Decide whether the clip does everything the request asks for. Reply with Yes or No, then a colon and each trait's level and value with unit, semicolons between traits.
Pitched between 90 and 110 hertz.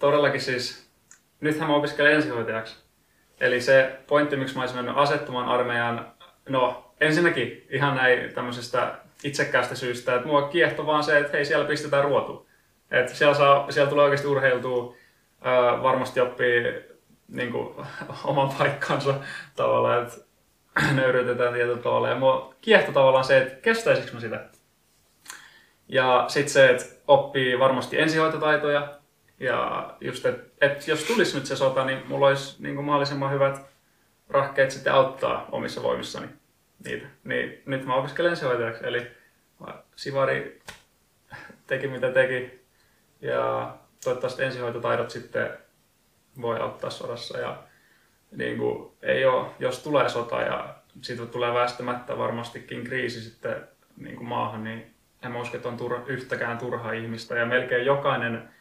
No: low, 135 Hz